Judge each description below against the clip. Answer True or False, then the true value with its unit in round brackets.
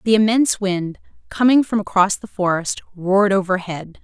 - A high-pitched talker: True (200 Hz)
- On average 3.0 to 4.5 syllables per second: False (5.1 syllables/s)